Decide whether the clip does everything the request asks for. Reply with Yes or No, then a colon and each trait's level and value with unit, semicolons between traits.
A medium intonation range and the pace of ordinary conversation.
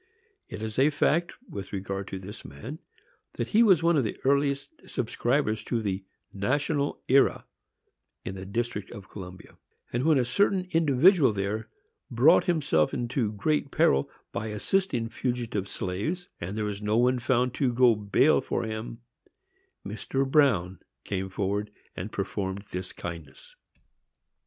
No: wide, 5.9 semitones; average, 145 wpm